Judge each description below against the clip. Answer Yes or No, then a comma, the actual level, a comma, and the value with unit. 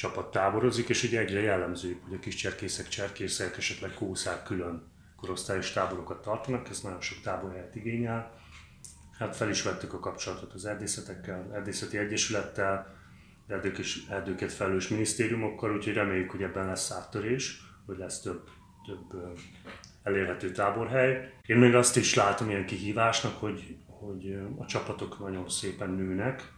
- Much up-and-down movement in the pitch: No, average, 3.0 semitones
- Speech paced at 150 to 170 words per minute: No, average, 140 wpm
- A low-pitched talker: Yes, low, 100 Hz